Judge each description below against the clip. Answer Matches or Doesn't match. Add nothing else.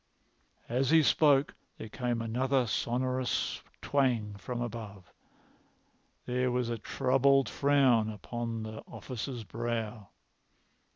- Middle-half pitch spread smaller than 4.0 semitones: Matches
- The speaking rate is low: Matches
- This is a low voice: Matches